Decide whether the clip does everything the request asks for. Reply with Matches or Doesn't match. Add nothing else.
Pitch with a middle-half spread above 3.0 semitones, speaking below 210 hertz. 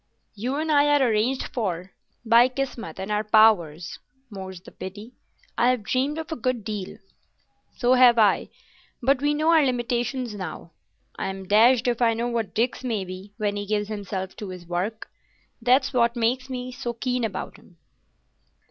Doesn't match